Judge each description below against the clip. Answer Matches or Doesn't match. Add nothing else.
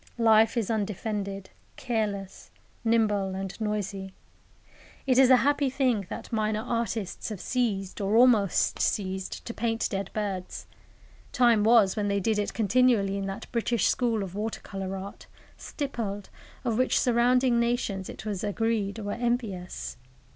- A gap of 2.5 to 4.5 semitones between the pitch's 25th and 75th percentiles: Matches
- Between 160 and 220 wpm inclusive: Doesn't match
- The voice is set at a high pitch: Matches